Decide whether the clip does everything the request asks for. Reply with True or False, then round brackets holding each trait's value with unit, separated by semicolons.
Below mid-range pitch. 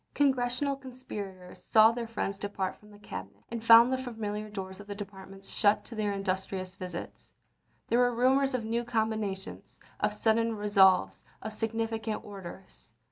False (215 Hz)